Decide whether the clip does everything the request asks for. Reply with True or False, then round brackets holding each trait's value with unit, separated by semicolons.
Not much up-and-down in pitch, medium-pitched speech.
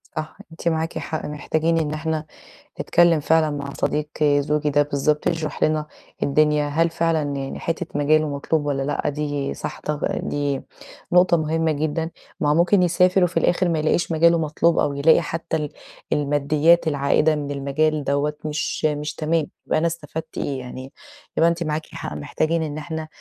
True (1.9 semitones; 155 Hz)